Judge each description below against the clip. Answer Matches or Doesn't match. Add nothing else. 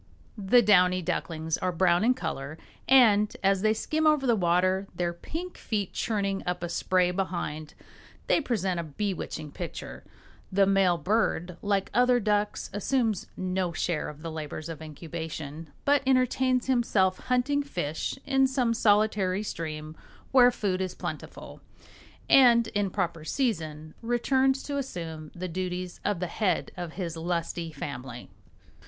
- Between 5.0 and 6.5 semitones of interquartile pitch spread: Matches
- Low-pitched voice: Doesn't match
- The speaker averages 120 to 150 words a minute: Matches